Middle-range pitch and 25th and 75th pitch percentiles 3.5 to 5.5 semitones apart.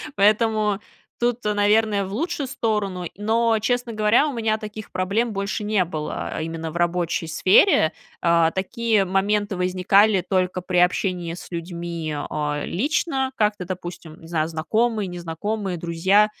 No: high, 195 Hz; average, 3.9 semitones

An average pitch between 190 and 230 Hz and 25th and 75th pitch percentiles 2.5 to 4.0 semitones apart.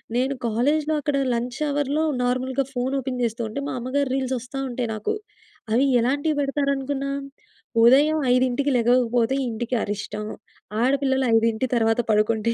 No: very high, 255 Hz; average, 3.0 semitones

